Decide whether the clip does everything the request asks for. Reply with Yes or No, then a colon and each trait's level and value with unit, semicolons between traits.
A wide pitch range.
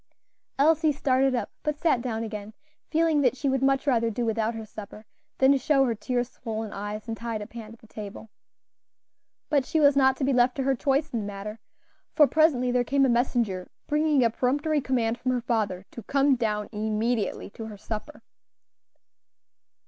No: average, 3.7 semitones